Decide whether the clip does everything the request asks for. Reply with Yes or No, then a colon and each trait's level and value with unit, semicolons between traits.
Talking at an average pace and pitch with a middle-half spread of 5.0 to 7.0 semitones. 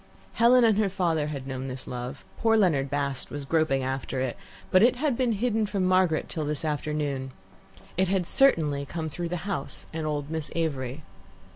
Yes: average, 185 wpm; wide, 5.6 semitones